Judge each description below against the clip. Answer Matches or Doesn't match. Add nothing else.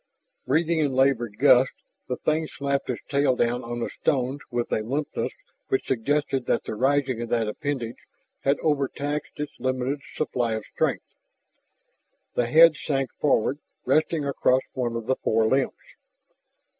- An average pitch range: Matches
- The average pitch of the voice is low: Matches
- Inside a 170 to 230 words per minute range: Doesn't match